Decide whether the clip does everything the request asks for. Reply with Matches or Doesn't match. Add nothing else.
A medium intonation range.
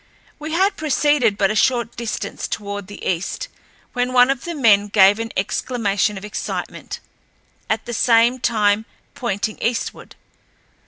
Matches